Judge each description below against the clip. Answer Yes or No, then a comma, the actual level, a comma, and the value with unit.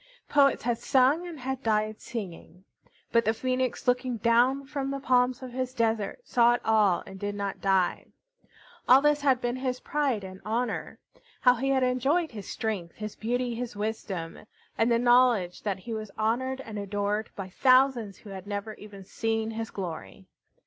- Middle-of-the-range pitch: No, high, 230 Hz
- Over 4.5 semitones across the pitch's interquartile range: No, average, 3.8 semitones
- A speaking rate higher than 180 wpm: No, average, 175 wpm